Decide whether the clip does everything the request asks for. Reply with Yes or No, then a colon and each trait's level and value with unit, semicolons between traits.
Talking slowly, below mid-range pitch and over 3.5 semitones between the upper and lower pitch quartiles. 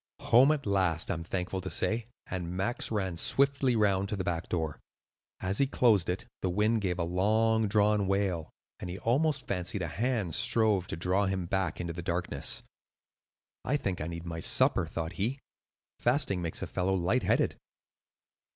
No: average, 180 wpm; very low, 95 Hz; average, 3.9 semitones